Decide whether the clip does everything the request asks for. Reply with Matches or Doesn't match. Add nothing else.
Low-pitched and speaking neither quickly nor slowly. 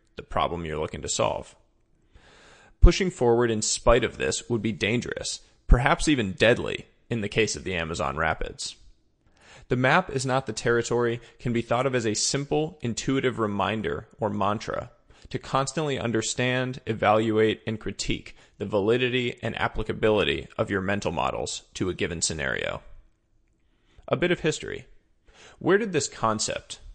Matches